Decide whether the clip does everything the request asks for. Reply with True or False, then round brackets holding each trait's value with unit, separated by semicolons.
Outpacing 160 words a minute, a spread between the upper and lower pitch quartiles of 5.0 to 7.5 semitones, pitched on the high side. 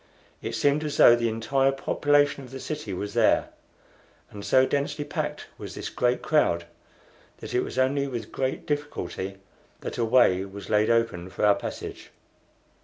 False (170 wpm; 5.4 semitones; 130 Hz)